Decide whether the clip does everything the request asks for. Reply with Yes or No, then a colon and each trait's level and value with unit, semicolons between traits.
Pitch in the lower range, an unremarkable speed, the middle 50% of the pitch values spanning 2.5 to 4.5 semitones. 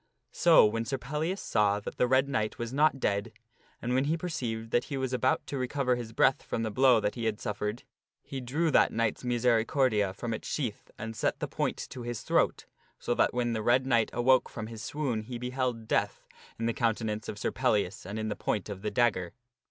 No: low, 120 Hz; fast, 220 wpm; average, 3.1 semitones